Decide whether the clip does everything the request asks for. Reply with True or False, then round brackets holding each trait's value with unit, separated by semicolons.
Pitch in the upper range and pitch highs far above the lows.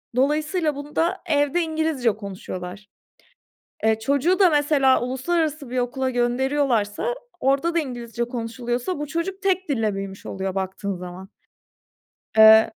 True (260 Hz; 5.9 semitones)